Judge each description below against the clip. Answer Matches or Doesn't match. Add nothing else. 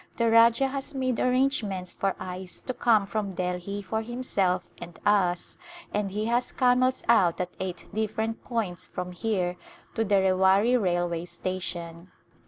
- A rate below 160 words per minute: Matches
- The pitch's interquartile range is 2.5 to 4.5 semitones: Matches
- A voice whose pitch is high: Matches